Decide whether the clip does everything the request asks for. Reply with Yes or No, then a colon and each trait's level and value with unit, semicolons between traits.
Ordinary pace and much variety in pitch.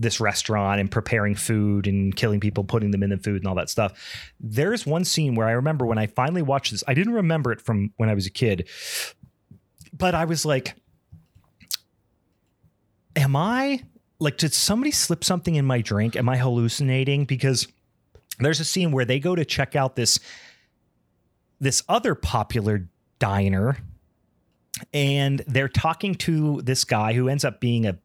Yes: average, 175 wpm; wide, 5.8 semitones